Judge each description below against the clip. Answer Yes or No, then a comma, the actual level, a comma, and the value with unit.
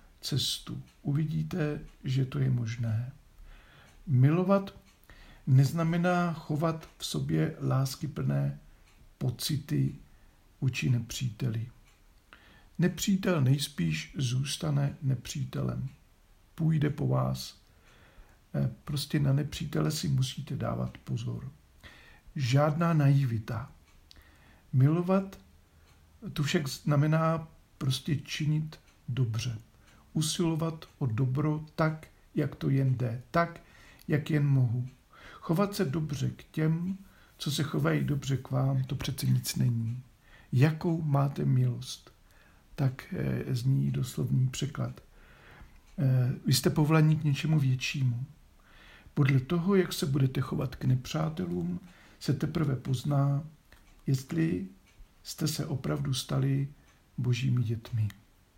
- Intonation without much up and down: No, average, 4.2 semitones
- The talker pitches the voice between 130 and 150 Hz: Yes, medium, 140 Hz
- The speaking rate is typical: No, slow, 100 wpm